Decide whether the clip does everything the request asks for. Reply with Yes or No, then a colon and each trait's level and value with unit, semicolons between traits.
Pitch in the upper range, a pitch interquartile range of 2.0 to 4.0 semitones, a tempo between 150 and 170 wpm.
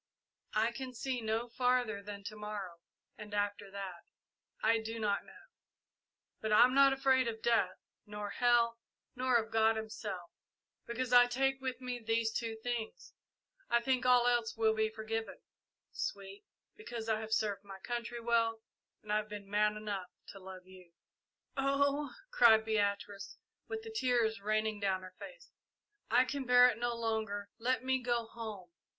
Yes: high, 225 Hz; average, 2.8 semitones; average, 165 wpm